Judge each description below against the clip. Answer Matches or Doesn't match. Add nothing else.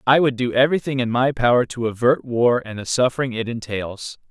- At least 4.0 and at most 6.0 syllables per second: Matches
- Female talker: Doesn't match